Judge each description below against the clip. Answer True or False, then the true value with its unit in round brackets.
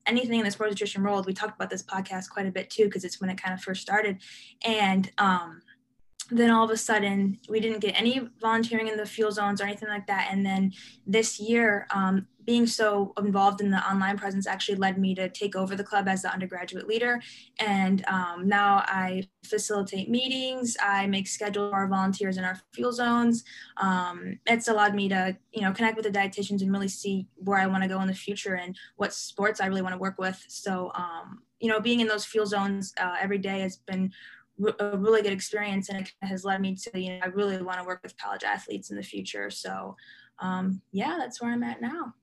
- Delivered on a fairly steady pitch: True (2.1 semitones)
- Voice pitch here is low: False (200 Hz)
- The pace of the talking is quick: True (225 wpm)